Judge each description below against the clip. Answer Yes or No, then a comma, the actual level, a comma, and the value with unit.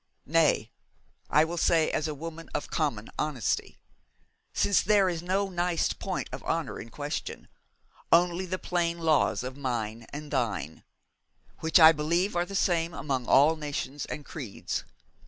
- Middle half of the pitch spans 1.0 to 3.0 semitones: No, average, 3.7 semitones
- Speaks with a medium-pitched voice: Yes, medium, 160 Hz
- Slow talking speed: No, average, 155 wpm